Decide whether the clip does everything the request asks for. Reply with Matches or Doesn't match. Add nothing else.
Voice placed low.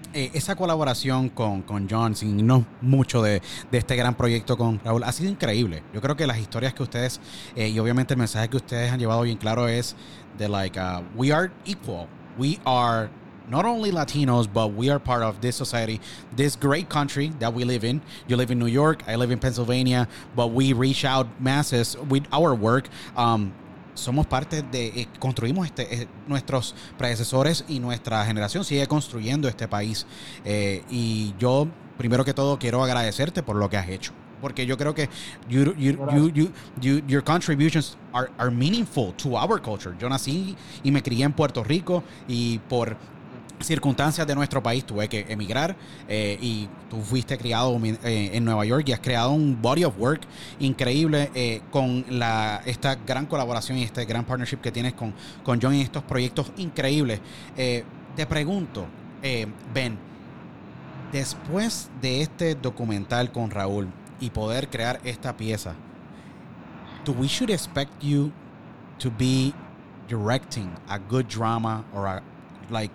Matches